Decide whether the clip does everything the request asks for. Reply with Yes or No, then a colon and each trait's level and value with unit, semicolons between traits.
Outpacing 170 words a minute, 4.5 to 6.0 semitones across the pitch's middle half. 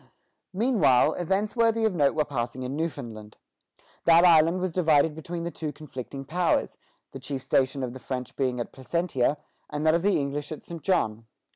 Yes: average, 180 wpm; average, 4.8 semitones